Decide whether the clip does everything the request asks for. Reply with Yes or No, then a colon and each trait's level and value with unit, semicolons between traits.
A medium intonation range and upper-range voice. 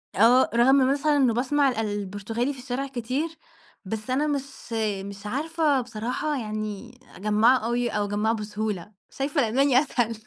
Yes: average, 4.2 semitones; high, 240 Hz